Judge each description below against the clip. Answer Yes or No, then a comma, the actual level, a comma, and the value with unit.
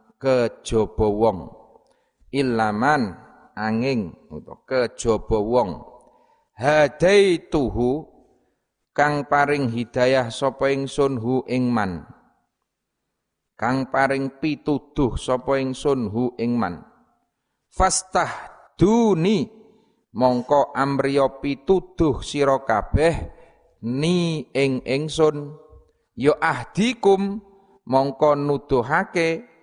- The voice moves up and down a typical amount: Yes, average, 4.3 semitones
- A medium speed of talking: No, slow, 75 wpm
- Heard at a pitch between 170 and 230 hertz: No, medium, 140 Hz